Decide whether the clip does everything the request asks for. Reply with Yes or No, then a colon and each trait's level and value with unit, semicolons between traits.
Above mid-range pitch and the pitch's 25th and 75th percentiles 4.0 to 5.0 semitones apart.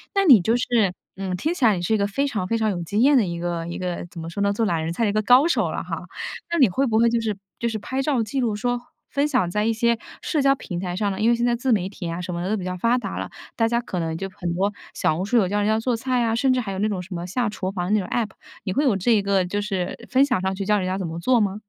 Yes: high, 210 Hz; average, 4.5 semitones